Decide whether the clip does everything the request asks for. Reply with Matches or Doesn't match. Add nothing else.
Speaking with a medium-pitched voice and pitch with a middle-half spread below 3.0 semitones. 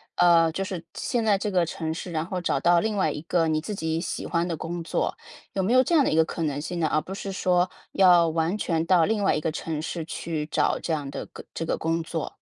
Matches